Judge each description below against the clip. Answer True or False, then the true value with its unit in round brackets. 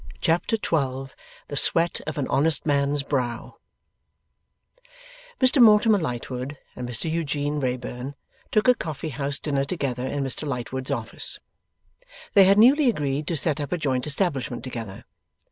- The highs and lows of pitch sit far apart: False (4.0 semitones)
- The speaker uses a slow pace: False (145 wpm)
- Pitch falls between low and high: True (145 Hz)